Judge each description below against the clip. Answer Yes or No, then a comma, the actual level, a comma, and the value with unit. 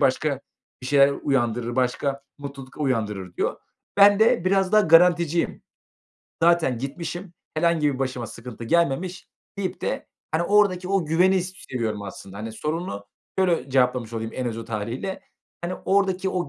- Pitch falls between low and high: Yes, medium, 145 Hz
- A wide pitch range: Yes, wide, 6.6 semitones